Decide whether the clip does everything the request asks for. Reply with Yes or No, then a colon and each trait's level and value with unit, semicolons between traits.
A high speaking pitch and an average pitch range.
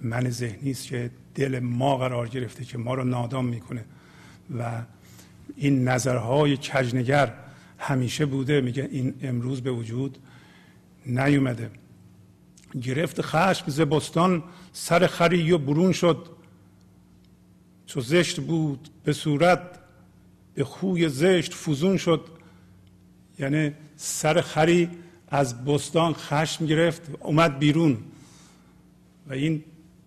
No: medium, 140 Hz; average, 4.4 semitones